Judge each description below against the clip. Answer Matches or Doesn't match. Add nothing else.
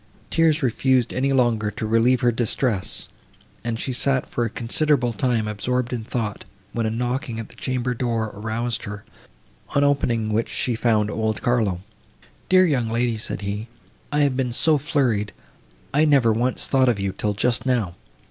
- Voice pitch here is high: Doesn't match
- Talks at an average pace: Matches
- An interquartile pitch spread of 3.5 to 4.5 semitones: Doesn't match